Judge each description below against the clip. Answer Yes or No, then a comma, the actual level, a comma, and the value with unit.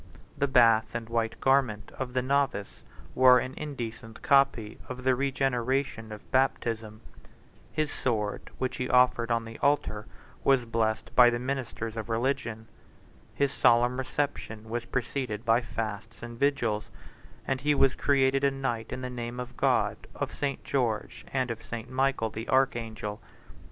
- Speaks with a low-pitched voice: Yes, low, 120 Hz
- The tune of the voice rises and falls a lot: No, average, 2.8 semitones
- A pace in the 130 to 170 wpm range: Yes, average, 155 wpm